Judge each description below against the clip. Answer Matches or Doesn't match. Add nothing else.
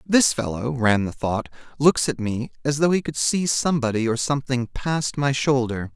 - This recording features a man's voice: Matches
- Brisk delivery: Doesn't match